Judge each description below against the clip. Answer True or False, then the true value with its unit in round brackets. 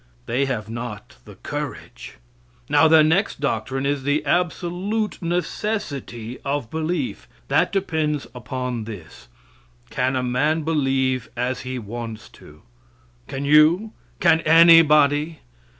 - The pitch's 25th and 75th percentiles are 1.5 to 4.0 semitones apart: False (4.4 semitones)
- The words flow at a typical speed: False (120 wpm)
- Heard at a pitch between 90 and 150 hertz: True (140 Hz)